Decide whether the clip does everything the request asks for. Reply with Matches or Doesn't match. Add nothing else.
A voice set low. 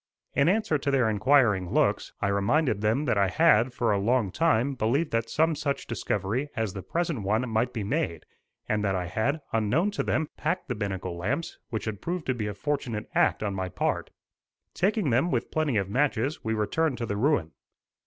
Matches